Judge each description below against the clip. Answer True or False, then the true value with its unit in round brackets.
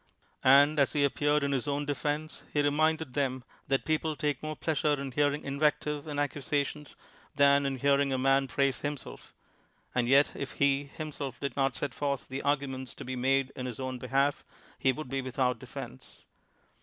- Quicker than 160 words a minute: True (190 wpm)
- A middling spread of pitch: False (1.6 semitones)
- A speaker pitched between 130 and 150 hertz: True (140 Hz)